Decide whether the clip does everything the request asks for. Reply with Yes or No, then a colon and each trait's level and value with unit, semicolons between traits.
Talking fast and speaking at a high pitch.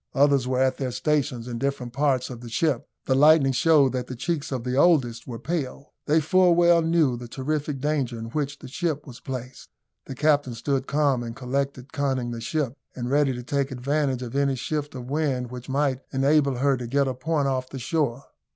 No: fast, 210 wpm; low, 135 Hz